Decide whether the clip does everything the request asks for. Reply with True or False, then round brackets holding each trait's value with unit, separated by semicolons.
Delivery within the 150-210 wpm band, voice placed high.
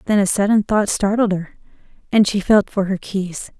True (200 wpm; 200 Hz)